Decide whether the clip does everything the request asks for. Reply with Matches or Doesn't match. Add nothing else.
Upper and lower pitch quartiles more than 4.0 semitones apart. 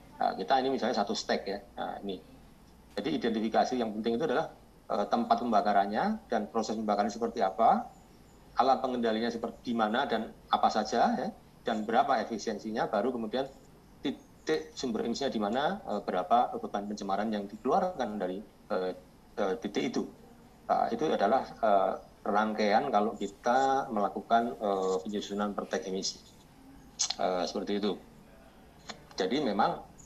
Doesn't match